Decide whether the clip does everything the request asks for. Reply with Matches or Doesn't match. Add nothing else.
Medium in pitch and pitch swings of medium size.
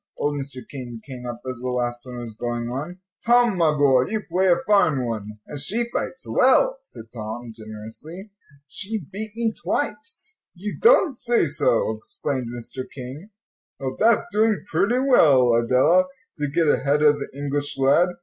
Doesn't match